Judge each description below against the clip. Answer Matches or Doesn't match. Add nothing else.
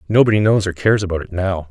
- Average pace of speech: Doesn't match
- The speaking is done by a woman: Doesn't match